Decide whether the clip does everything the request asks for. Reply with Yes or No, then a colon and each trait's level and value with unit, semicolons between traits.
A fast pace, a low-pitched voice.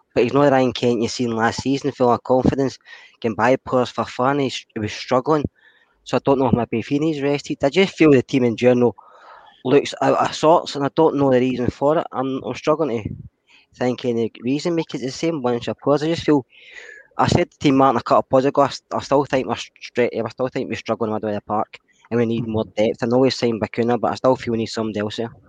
Yes: fast, 255 wpm; low, 125 Hz